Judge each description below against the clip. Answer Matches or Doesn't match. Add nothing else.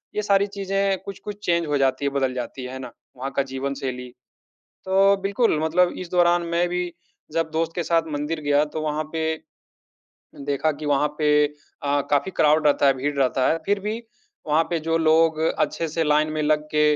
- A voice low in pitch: Doesn't match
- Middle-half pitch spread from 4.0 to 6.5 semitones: Doesn't match